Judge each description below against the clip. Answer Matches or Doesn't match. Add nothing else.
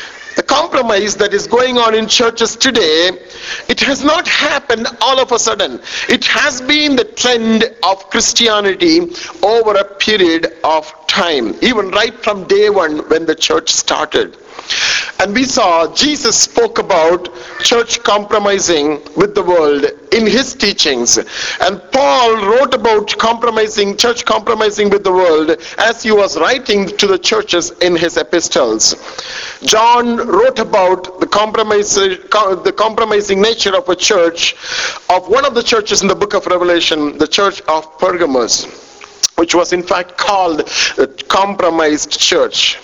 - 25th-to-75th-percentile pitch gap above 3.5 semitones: Matches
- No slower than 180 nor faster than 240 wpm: Doesn't match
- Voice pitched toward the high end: Matches